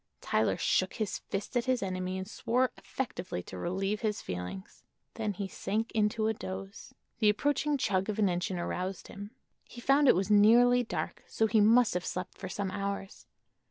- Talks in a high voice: Yes, high, 205 Hz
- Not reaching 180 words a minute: No, average, 185 wpm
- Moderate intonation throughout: Yes, average, 3.4 semitones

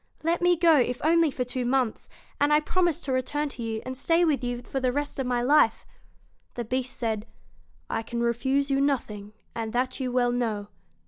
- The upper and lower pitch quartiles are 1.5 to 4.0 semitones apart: Yes, average, 3.2 semitones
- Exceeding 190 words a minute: Yes, average, 200 wpm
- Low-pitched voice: No, very high, 255 Hz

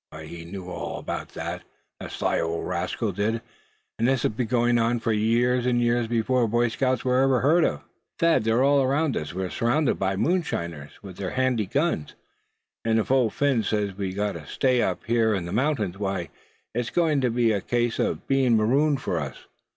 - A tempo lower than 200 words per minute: No, fast, 205 wpm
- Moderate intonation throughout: Yes, average, 4.4 semitones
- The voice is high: No, low, 115 Hz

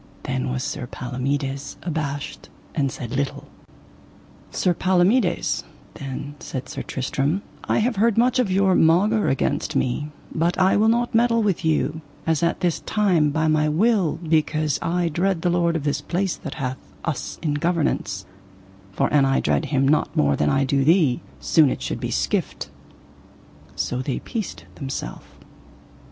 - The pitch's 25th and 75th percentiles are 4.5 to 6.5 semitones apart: Yes, average, 5.2 semitones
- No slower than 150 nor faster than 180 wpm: Yes, average, 160 wpm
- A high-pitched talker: No, medium, 155 Hz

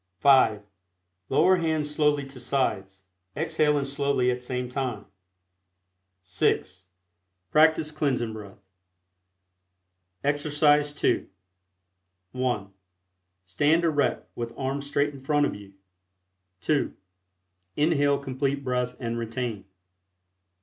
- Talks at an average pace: No, slow, 95 wpm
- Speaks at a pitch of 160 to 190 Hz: No, low, 135 Hz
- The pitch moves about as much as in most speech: Yes, average, 3.5 semitones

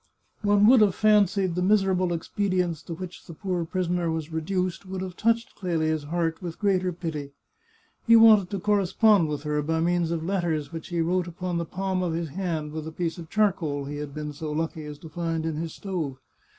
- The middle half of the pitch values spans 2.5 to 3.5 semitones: Yes, average, 2.9 semitones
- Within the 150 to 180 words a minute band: No, fast, 205 wpm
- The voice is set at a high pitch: No, medium, 175 Hz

